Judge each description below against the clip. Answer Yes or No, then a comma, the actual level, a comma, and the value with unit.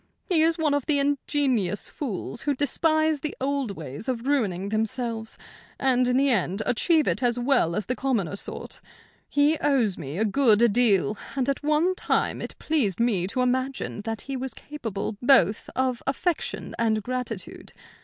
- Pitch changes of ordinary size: Yes, average, 4.7 semitones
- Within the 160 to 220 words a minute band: Yes, average, 170 wpm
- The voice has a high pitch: Yes, very high, 250 Hz